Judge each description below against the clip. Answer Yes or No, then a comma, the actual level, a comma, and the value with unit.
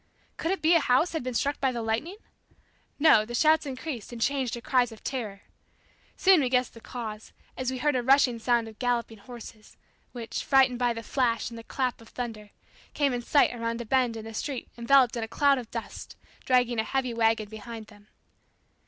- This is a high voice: Yes, high, 245 Hz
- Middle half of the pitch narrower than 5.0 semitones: Yes, average, 2.8 semitones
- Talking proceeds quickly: Yes, fast, 210 wpm